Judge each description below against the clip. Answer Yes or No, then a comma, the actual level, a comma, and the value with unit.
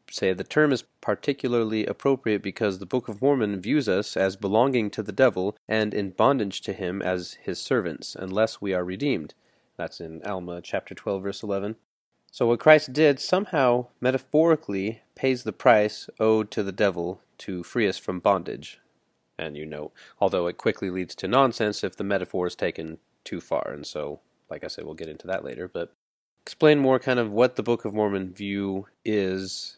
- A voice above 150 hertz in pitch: No, low, 105 Hz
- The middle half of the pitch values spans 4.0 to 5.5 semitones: Yes, average, 4.8 semitones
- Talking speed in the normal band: Yes, average, 185 wpm